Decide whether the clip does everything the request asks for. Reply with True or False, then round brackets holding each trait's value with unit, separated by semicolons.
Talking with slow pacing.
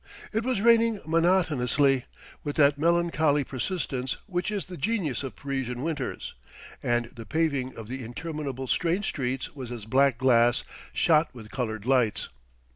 False (145 wpm)